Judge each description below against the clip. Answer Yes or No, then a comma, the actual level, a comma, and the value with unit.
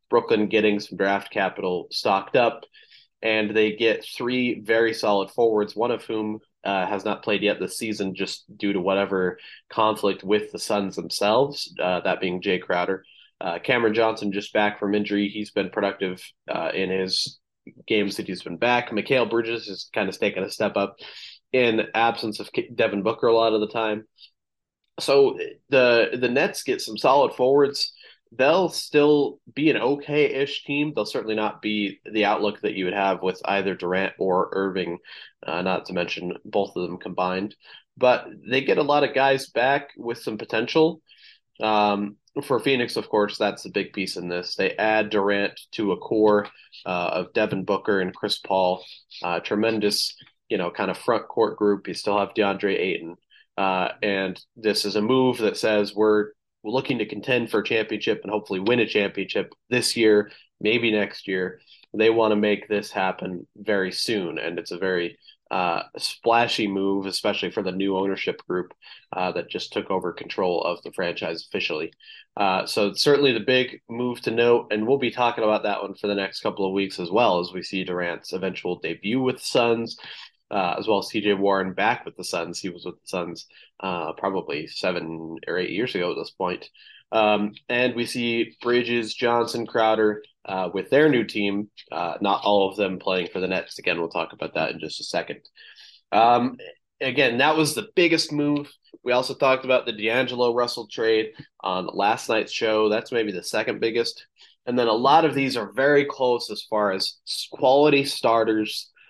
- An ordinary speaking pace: Yes, average, 190 wpm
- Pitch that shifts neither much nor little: Yes, average, 3.7 semitones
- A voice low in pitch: Yes, low, 105 Hz